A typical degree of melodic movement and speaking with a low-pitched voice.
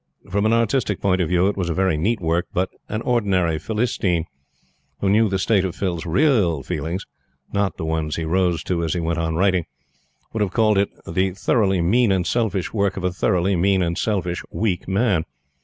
Yes: average, 3.2 semitones; very low, 95 Hz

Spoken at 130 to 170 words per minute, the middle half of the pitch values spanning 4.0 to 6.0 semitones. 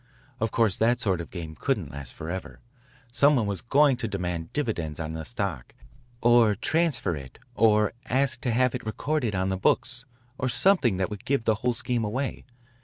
No: average, 185 wpm; wide, 5.4 semitones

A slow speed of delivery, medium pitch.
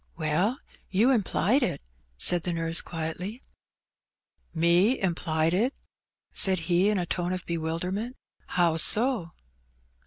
Yes: slow, 120 wpm; medium, 180 Hz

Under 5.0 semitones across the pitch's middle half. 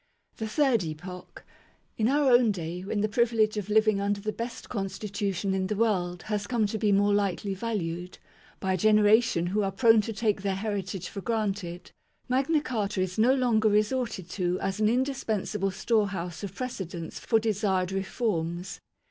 Yes: average, 2.9 semitones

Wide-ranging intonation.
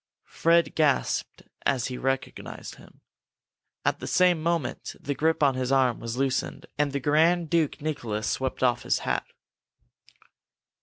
No: average, 3.8 semitones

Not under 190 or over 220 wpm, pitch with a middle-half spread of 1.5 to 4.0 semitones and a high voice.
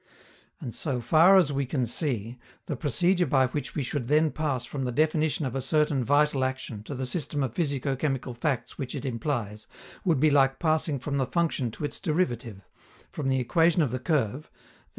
No: average, 200 wpm; average, 3.4 semitones; medium, 140 Hz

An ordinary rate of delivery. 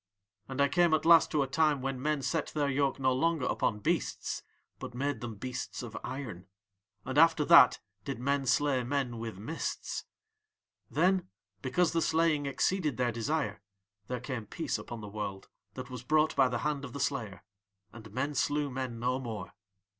Yes: average, 180 wpm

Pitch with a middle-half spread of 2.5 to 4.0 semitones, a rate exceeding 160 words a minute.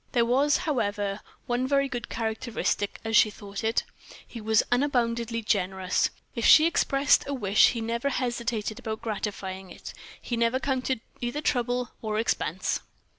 No: average, 3.0 semitones; average, 150 wpm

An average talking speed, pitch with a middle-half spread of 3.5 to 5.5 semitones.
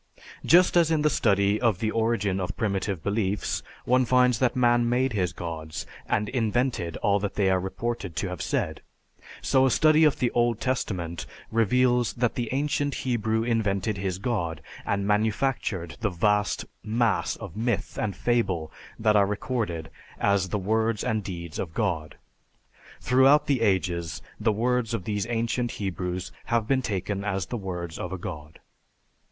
Yes: average, 165 wpm; average, 4.3 semitones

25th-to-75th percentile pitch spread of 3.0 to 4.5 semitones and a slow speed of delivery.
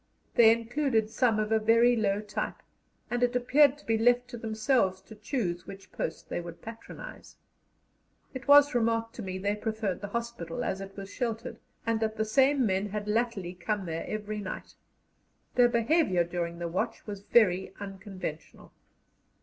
No: average, 3.5 semitones; average, 170 wpm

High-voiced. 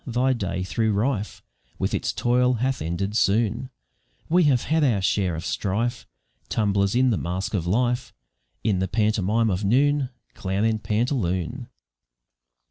No: low, 110 Hz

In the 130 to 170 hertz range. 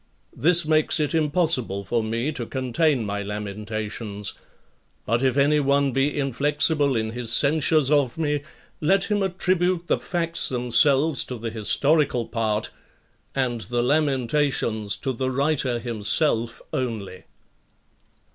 Yes: low, 135 Hz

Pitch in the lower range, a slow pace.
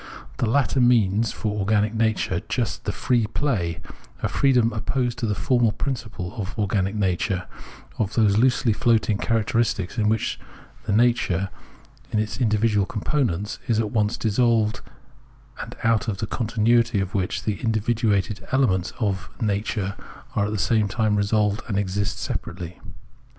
No: low, 110 Hz; average, 150 wpm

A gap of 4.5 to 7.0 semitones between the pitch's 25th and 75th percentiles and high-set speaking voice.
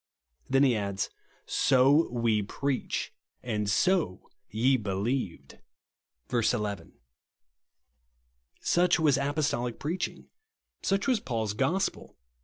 No: wide, 5.5 semitones; low, 125 Hz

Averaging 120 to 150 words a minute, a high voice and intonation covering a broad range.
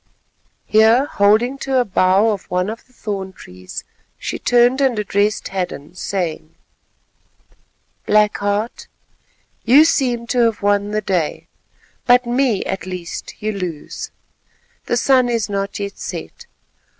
No: slow, 135 wpm; high, 210 Hz; average, 4.0 semitones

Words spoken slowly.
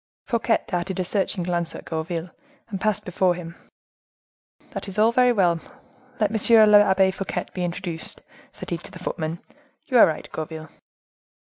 No: average, 155 wpm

